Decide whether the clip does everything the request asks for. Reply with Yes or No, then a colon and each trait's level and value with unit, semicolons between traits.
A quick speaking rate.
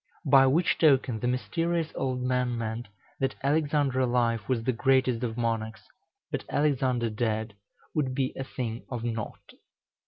No: average, 150 wpm